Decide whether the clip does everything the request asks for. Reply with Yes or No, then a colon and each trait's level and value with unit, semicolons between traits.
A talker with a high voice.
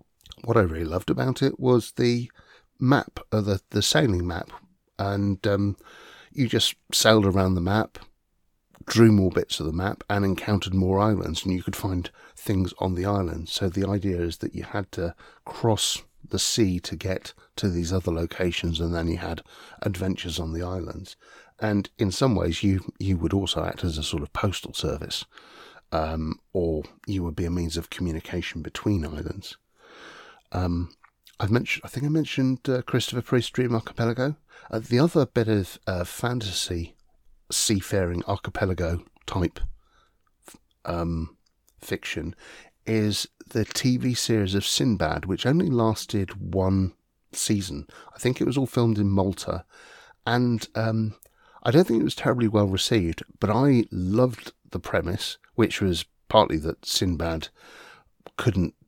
No: low, 100 Hz